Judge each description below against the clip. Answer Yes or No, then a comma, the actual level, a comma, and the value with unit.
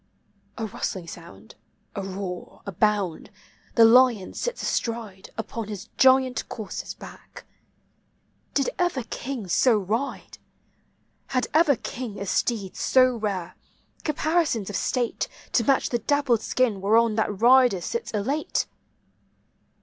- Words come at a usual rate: No, slow, 125 wpm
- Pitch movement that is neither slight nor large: Yes, average, 4.5 semitones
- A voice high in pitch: Yes, high, 225 Hz